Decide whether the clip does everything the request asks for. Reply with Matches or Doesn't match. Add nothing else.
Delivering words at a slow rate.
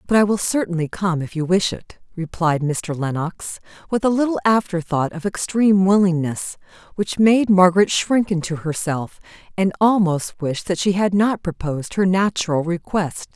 Doesn't match